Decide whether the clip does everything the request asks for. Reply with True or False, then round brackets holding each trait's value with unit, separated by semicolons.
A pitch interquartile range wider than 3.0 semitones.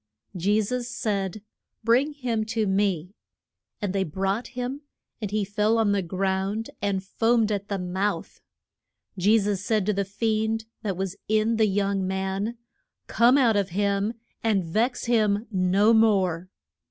False (2.5 semitones)